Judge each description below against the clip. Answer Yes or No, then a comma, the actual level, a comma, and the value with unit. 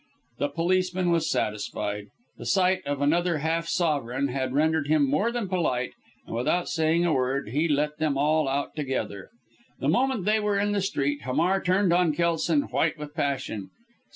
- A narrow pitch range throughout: No, average, 4.4 semitones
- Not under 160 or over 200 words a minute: Yes, average, 175 wpm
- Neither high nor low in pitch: Yes, medium, 155 Hz